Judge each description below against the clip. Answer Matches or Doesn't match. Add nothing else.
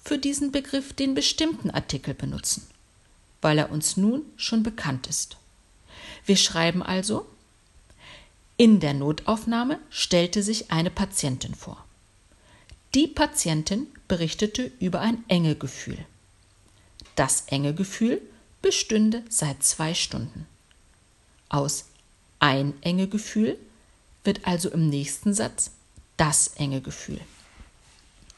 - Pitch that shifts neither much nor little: Doesn't match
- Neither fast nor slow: Doesn't match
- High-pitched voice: Doesn't match